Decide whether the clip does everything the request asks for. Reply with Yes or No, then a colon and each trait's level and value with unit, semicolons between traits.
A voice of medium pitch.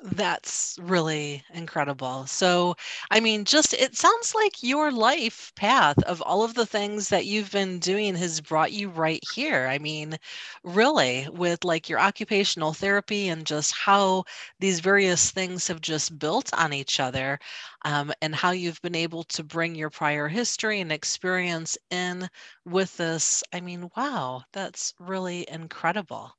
Yes: medium, 175 Hz